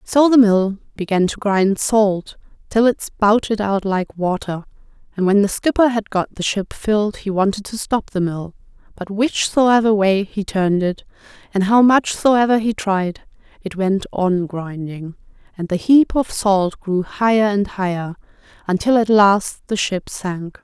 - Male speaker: No, female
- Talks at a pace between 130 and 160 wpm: No, average, 170 wpm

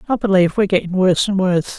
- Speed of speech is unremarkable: No, fast, 235 wpm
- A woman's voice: Yes, female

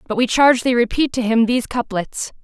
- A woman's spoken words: Yes, female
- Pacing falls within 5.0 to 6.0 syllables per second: Yes, 5.9 syllables/s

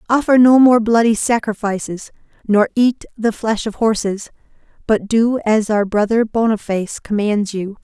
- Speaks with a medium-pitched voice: No, high, 220 Hz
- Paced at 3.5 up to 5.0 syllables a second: Yes, 4.7 syllables/s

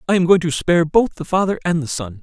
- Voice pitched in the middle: Yes, medium, 165 Hz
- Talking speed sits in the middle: No, fast, 295 wpm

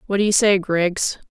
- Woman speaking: Yes, female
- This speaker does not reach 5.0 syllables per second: Yes, 4.7 syllables/s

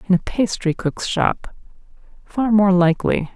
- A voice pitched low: No, high, 190 Hz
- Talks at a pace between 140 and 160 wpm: Yes, average, 145 wpm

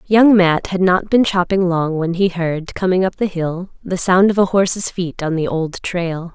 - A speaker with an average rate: No, fast, 225 wpm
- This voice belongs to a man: No, female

